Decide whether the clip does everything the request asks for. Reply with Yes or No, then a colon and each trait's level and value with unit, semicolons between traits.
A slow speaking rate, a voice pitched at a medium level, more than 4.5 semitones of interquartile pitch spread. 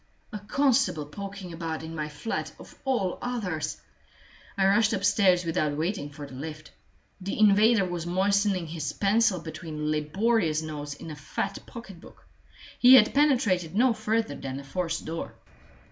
No: average, 150 wpm; medium, 180 Hz; average, 5.3 semitones